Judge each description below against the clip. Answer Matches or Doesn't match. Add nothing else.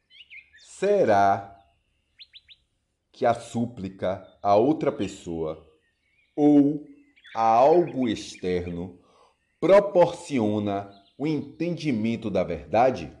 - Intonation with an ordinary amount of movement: Doesn't match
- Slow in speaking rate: Matches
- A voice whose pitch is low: Matches